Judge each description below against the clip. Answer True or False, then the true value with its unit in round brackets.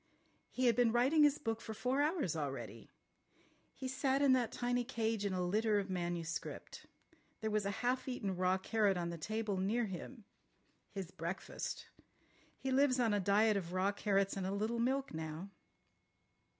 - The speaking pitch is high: True (215 Hz)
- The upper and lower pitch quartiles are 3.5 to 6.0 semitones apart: True (4.7 semitones)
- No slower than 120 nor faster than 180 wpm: True (175 wpm)